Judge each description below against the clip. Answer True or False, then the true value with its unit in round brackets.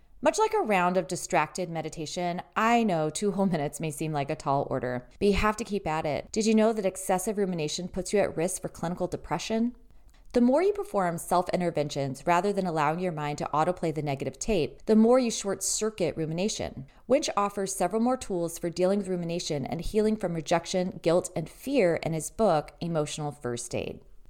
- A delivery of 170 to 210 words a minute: True (200 wpm)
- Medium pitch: True (180 Hz)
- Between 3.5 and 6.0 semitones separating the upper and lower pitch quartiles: True (4.5 semitones)